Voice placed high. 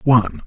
No: low, 115 Hz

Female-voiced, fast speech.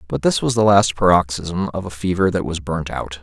No: male; fast, 240 wpm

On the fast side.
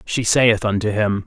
No: average, 190 wpm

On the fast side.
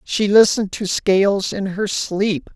No: average, 165 wpm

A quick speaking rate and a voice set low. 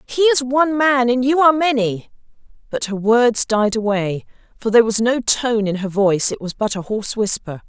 No: fast, 210 wpm; high, 235 Hz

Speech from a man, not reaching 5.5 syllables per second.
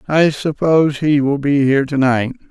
Yes: male; 5.0 syllables/s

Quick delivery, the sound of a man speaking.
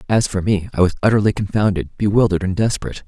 No: average, 195 wpm; male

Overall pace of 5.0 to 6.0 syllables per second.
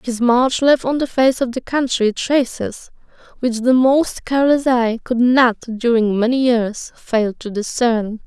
No: 4.0 syllables/s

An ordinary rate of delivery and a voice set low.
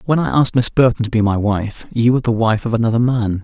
No: fast, 280 wpm; low, 115 Hz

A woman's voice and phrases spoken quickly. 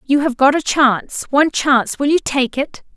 Yes: female; fast, 225 wpm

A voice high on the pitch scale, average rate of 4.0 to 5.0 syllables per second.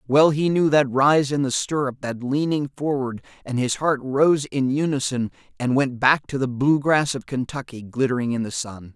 No: low, 135 Hz; 4.7 syllables/s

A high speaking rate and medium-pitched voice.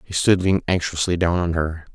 No: fast, 215 wpm; very low, 85 Hz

